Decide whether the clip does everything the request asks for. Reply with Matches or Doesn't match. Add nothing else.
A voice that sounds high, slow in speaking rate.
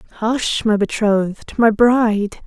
Matches